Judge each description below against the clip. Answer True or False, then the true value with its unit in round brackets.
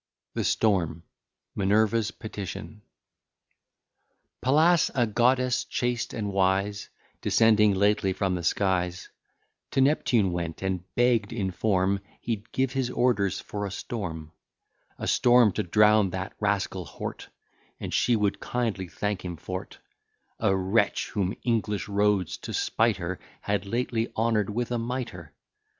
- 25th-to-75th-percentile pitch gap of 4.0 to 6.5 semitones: False (3.6 semitones)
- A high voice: False (105 Hz)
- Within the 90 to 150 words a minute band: True (135 wpm)